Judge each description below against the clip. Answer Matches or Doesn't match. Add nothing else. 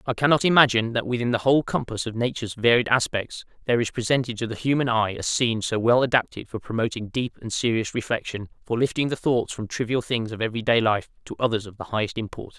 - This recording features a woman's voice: Doesn't match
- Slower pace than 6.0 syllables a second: Doesn't match